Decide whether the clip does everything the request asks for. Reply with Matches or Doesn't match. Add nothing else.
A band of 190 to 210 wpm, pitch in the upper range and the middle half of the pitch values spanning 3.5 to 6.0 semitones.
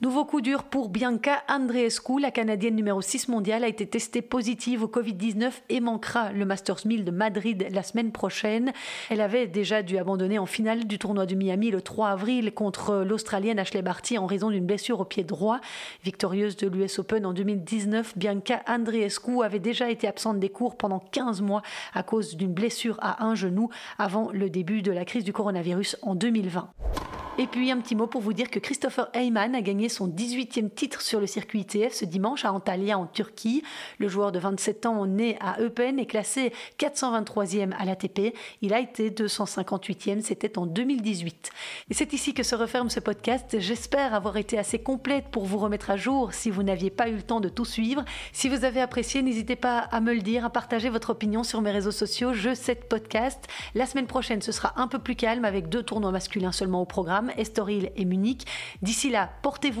Doesn't match